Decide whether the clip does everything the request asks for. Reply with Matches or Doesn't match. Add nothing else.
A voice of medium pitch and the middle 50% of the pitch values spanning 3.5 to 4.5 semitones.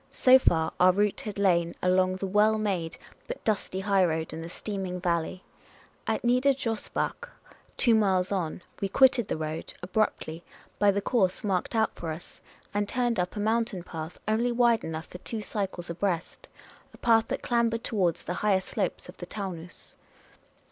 Doesn't match